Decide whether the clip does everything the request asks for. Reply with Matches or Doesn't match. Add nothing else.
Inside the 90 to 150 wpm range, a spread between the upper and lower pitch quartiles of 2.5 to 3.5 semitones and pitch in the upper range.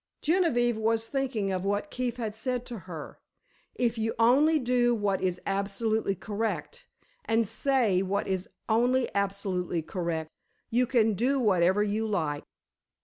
Doesn't match